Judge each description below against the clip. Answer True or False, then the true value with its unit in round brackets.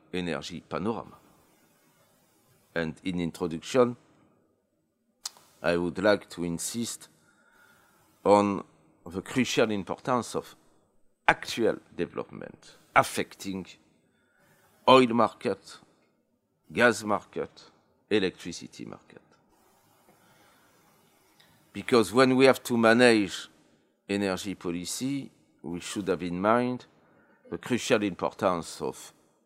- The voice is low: True (100 Hz)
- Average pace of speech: False (85 wpm)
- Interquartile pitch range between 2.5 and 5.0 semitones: False (5.6 semitones)